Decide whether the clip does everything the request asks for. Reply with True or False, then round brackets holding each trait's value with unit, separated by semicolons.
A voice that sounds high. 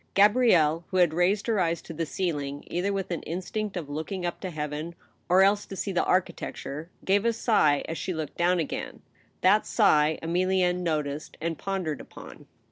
False (175 Hz)